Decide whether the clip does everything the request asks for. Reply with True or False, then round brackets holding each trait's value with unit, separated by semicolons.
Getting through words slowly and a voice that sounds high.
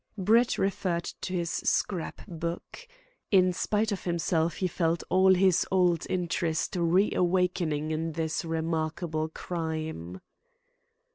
False (120 wpm; 170 Hz)